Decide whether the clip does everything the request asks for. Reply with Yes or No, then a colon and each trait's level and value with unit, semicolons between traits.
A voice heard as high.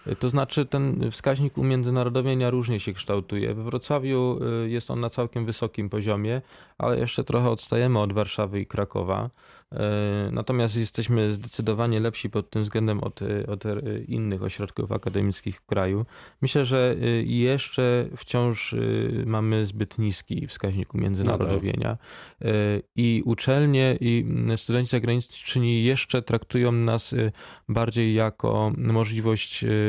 No: low, 115 Hz